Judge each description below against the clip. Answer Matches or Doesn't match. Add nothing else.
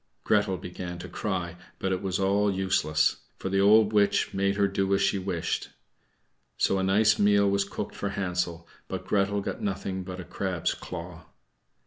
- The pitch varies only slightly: Matches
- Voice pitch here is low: Matches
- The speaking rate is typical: Matches